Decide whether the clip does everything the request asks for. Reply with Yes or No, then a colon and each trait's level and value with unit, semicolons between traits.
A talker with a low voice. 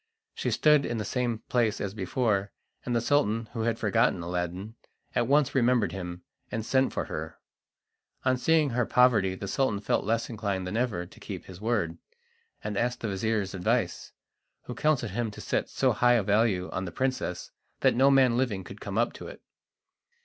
Yes: low, 115 Hz